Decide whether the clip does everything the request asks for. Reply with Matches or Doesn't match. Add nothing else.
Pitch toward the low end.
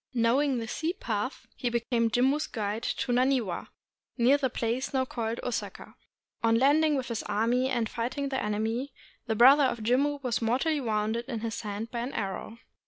Doesn't match